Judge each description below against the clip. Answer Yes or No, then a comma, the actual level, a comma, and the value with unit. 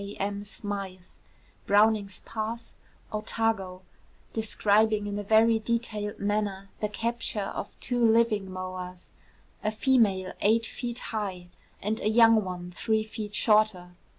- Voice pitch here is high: Yes, high, 210 Hz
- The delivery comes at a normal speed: No, slow, 125 wpm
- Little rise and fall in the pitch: Yes, narrow, 2.1 semitones